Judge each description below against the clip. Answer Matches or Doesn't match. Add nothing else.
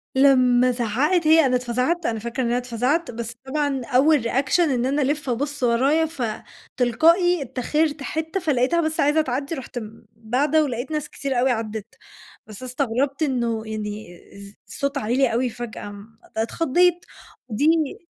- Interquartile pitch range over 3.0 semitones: Matches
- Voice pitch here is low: Doesn't match